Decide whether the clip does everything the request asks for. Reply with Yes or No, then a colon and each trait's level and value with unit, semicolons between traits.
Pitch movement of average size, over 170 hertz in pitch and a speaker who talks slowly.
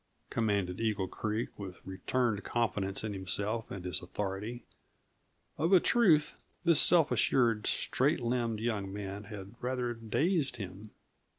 No: average, 3.9 semitones; low, 110 Hz; slow, 130 wpm